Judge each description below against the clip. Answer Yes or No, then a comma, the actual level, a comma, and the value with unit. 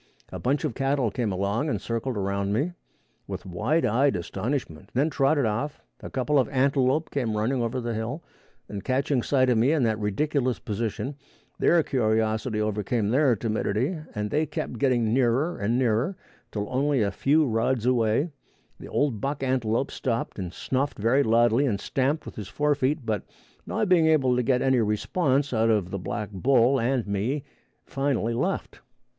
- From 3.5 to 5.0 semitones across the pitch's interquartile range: Yes, average, 4.2 semitones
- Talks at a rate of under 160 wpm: No, average, 175 wpm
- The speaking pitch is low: Yes, low, 125 Hz